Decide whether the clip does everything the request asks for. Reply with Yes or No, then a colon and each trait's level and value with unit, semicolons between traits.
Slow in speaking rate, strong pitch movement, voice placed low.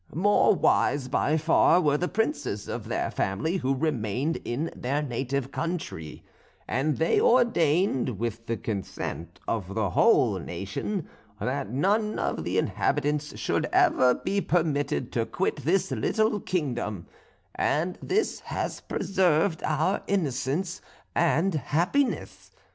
No: slow, 125 wpm; wide, 6.5 semitones; medium, 150 Hz